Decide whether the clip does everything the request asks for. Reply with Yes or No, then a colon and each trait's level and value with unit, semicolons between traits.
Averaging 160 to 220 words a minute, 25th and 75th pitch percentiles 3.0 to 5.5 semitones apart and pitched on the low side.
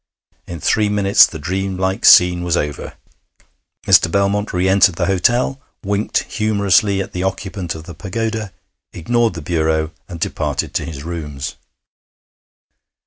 No: average, 140 wpm; average, 3.3 semitones; very low, 95 Hz